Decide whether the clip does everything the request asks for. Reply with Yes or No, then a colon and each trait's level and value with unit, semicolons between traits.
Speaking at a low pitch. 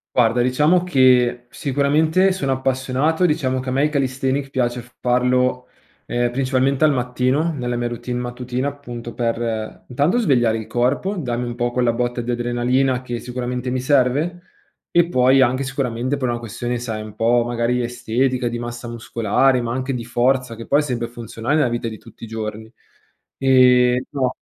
Yes: low, 125 Hz